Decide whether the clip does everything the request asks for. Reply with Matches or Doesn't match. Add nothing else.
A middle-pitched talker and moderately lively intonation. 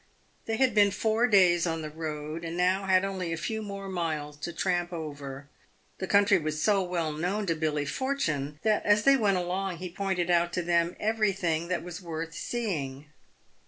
Matches